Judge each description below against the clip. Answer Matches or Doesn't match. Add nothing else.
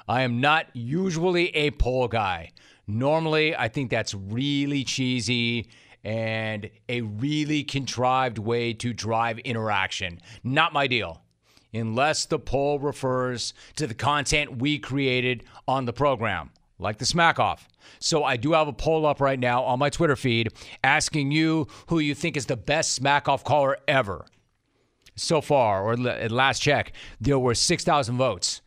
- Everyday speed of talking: Matches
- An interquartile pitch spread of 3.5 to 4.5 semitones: Matches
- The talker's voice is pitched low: Matches